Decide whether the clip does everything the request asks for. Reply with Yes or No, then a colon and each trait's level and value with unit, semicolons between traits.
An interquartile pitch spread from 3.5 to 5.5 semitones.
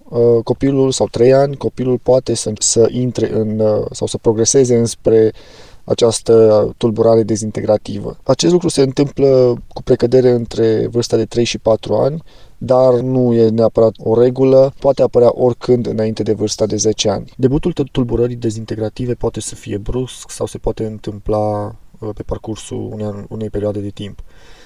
No: average, 2.7 semitones